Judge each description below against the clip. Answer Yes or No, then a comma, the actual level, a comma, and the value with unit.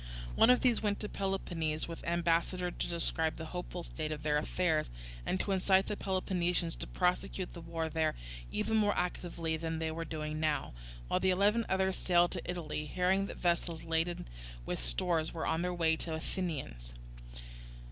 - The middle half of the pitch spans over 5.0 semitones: No, narrow, 2.6 semitones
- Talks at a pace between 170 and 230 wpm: Yes, average, 180 wpm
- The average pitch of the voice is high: No, medium, 170 Hz